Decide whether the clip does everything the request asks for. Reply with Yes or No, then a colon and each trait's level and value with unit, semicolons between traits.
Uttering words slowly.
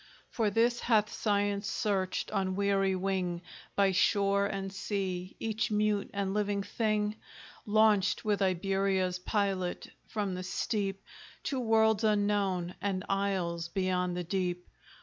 Yes: slow, 130 wpm